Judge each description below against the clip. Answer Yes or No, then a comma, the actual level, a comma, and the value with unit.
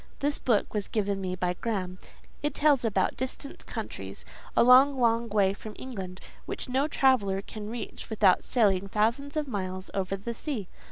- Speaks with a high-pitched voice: Yes, high, 215 Hz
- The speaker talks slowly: No, average, 170 wpm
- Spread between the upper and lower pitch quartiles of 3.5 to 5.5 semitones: Yes, average, 5.0 semitones